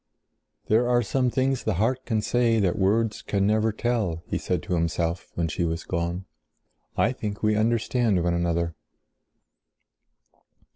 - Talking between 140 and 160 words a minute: Yes, average, 150 wpm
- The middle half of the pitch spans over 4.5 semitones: Yes, average, 5.3 semitones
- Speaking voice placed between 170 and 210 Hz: No, low, 105 Hz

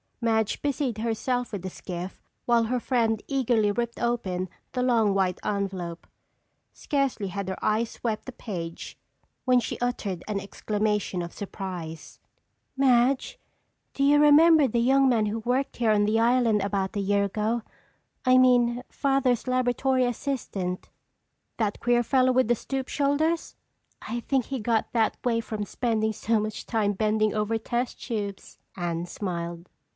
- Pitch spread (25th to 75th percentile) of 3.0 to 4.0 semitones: Yes, average, 3.7 semitones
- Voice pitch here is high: Yes, high, 225 Hz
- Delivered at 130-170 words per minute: Yes, average, 150 wpm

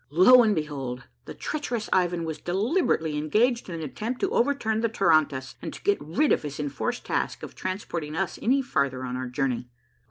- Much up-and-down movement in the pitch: Yes, wide, 7.3 semitones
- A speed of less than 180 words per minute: No, average, 190 wpm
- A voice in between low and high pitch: Yes, medium, 170 Hz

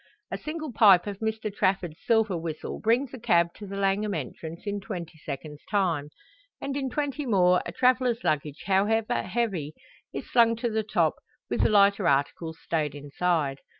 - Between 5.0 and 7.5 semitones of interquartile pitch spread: Yes, wide, 5.5 semitones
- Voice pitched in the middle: No, high, 195 Hz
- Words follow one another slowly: No, average, 170 wpm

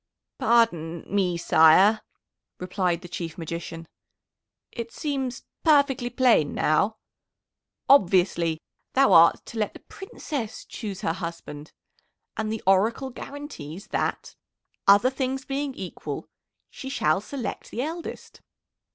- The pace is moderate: No, slow, 115 wpm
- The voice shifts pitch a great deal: Yes, wide, 7.5 semitones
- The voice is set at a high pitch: Yes, high, 210 Hz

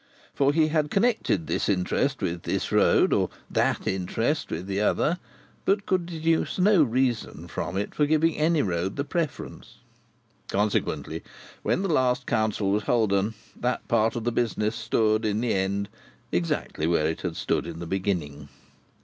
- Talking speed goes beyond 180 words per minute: No, average, 165 wpm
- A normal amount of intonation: No, wide, 7.6 semitones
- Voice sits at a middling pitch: No, low, 110 Hz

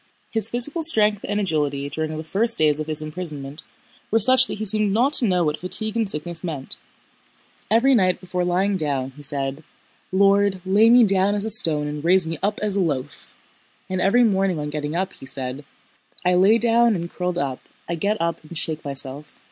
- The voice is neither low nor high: Yes, medium, 180 Hz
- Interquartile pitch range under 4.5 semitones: No, wide, 5.6 semitones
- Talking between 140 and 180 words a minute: No, fast, 205 wpm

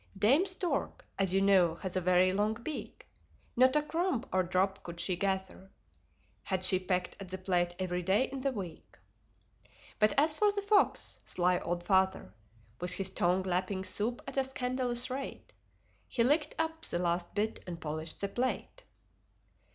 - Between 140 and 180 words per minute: Yes, average, 170 wpm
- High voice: Yes, high, 195 Hz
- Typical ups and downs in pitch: No, wide, 6.1 semitones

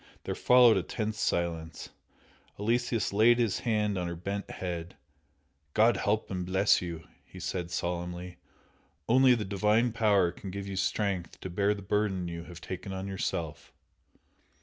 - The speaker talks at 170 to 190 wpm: No, average, 155 wpm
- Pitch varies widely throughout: No, average, 3.3 semitones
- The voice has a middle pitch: No, very low, 95 Hz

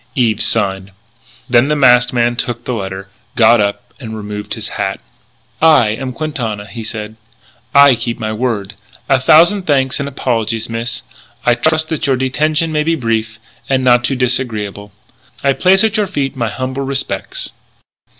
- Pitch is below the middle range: Yes, low, 125 Hz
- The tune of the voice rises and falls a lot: No, average, 4.0 semitones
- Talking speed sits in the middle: Yes, average, 160 wpm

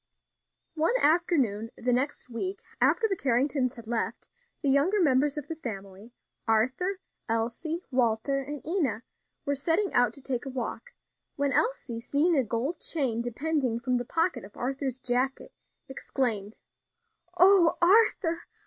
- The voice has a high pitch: Yes, very high, 270 Hz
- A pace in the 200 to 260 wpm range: No, average, 140 wpm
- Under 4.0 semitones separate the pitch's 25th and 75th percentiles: No, wide, 5.5 semitones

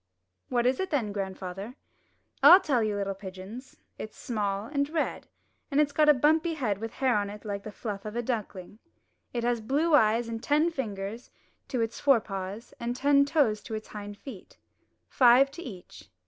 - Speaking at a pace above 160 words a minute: Yes, average, 190 wpm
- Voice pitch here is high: Yes, high, 230 Hz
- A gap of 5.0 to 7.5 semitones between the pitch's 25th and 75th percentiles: Yes, average, 5.3 semitones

